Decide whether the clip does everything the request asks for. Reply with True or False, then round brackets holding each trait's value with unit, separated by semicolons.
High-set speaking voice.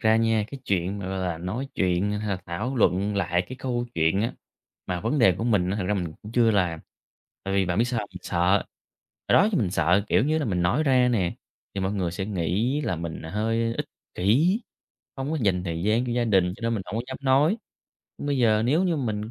False (105 Hz)